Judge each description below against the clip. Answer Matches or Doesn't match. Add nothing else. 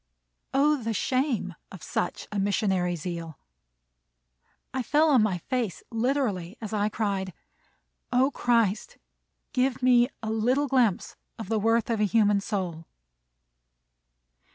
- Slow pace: Matches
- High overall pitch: Matches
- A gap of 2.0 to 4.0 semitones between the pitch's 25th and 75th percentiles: Doesn't match